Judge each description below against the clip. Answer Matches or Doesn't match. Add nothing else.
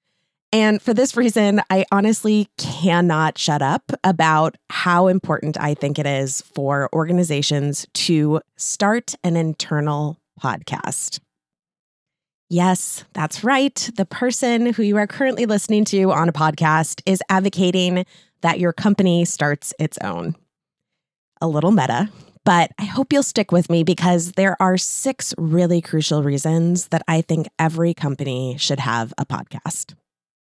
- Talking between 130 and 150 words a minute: Matches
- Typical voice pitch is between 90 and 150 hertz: Doesn't match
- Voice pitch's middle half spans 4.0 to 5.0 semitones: Matches